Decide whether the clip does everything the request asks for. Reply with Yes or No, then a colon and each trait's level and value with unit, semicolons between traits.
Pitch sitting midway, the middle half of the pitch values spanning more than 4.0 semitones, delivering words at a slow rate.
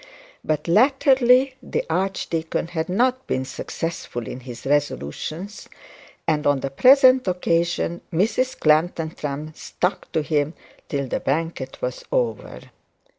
Yes: medium, 165 Hz; wide, 5.6 semitones; slow, 120 wpm